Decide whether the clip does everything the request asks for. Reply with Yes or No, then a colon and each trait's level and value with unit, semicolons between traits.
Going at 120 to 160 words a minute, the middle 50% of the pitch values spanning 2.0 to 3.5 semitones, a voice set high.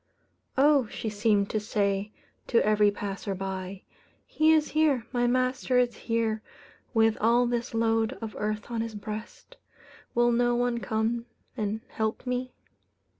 Yes: average, 140 wpm; narrow, 2.5 semitones; high, 225 Hz